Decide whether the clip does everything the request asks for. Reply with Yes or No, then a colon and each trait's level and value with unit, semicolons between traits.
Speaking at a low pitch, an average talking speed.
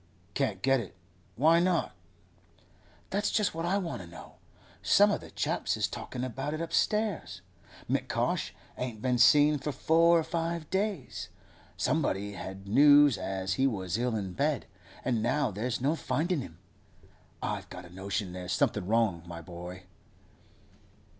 Yes: low, 125 Hz; average, 155 wpm